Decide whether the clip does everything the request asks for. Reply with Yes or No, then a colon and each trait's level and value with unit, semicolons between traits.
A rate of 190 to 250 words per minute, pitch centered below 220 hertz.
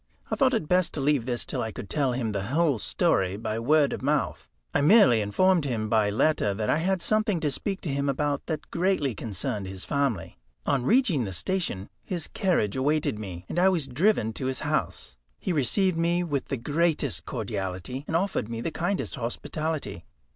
Yes: average, 195 wpm; medium, 140 Hz